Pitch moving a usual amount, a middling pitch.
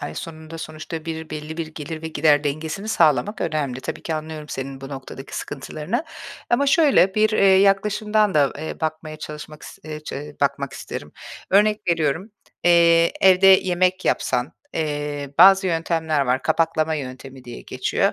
Yes: average, 3.9 semitones; medium, 160 Hz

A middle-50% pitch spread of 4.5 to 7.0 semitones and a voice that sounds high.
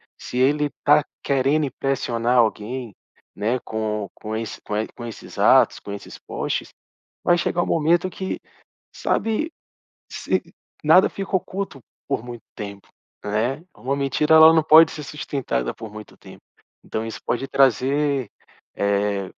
No: wide, 5.5 semitones; low, 130 Hz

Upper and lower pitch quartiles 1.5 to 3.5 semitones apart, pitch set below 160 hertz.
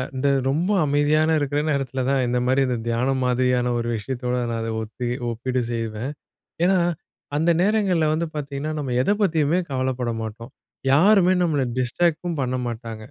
No: average, 4.2 semitones; low, 135 Hz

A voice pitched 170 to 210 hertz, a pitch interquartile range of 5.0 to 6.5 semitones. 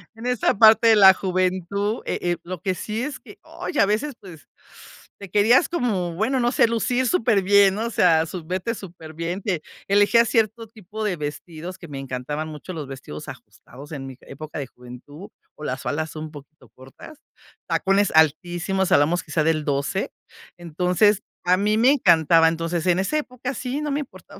Yes: medium, 185 Hz; wide, 5.5 semitones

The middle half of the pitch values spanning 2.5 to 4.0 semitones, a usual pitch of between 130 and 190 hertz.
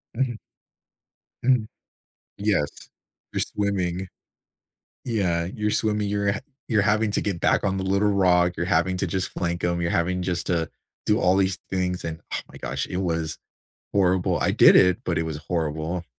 No: average, 2.8 semitones; very low, 90 Hz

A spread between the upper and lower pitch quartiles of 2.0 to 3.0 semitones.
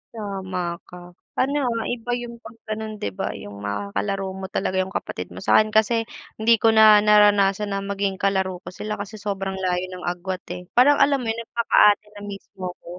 Yes: average, 2.7 semitones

